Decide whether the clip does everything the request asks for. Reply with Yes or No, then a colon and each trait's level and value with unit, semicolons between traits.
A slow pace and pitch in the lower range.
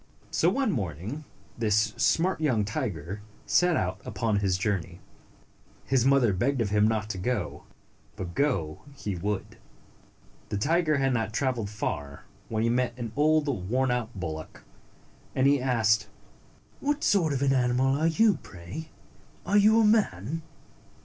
No: average, 150 wpm; low, 120 Hz